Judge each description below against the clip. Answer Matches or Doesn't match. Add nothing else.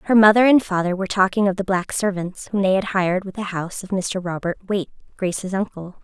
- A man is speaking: Doesn't match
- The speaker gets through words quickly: Matches